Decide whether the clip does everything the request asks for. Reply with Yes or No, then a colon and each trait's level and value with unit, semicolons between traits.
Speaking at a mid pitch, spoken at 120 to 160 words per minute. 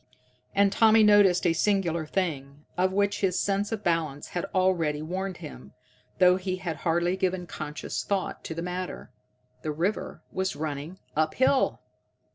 Yes: medium, 180 Hz; average, 155 wpm